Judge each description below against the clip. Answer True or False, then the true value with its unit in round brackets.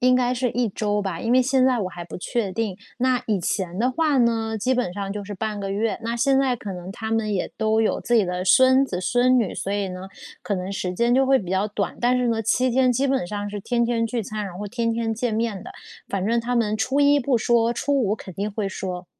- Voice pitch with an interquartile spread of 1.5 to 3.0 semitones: False (3.8 semitones)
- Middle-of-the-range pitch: False (225 Hz)